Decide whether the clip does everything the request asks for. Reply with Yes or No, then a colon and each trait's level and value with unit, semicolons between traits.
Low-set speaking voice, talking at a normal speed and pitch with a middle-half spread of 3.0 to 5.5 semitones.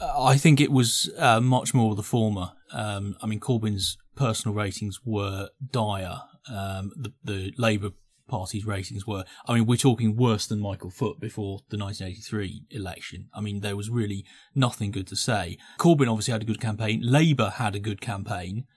Yes: low, 110 Hz; average, 180 wpm; average, 3.5 semitones